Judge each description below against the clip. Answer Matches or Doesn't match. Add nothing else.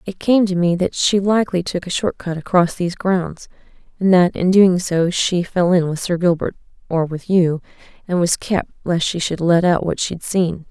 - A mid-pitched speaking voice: Matches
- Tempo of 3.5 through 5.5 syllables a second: Matches